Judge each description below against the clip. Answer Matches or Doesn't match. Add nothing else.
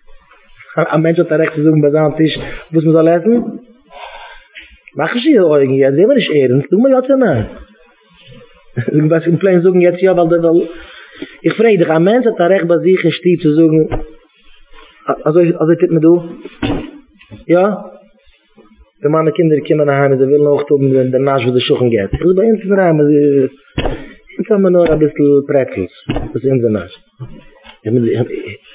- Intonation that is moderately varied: Matches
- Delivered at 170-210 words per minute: Doesn't match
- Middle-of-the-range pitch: Matches